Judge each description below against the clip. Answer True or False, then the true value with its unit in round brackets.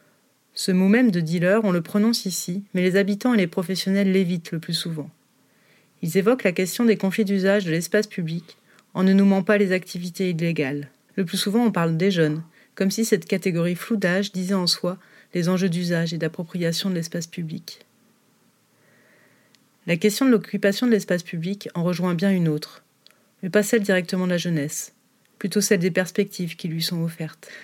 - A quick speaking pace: False (190 wpm)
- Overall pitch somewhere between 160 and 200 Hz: True (185 Hz)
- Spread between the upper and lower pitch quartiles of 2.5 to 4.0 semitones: True (2.9 semitones)